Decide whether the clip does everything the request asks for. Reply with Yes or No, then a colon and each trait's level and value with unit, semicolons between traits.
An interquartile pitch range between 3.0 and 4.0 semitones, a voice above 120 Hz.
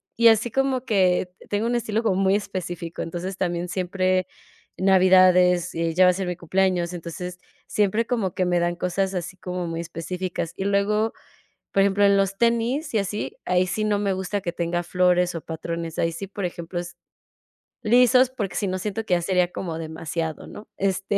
No: narrow, 2.6 semitones; medium, 185 Hz